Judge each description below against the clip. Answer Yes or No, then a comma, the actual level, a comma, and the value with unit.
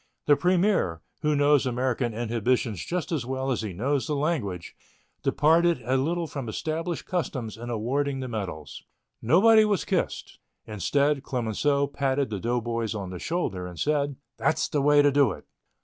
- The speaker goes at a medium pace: Yes, average, 165 wpm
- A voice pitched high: No, low, 135 Hz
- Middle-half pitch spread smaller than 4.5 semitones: No, average, 4.8 semitones